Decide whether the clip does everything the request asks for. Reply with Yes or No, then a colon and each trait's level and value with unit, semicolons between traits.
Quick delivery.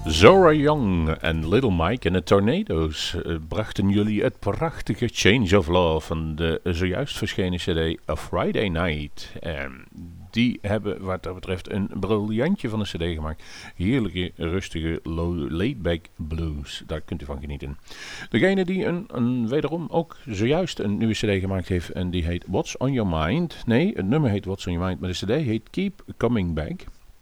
No: average, 175 wpm